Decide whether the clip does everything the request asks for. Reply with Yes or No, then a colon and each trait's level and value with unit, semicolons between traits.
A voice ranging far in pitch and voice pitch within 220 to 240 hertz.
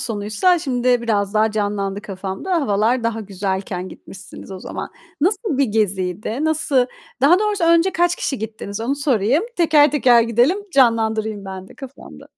Yes: wide, 5.9 semitones; high, 230 Hz